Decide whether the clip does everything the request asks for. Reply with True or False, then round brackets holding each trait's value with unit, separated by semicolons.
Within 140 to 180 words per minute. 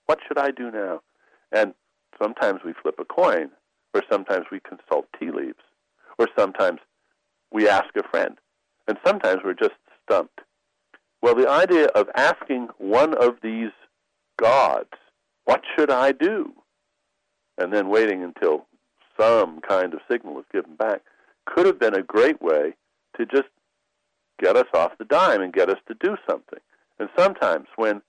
True (160 wpm)